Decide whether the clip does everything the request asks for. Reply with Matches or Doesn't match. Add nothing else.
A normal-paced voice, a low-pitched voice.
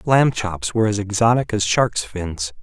Matches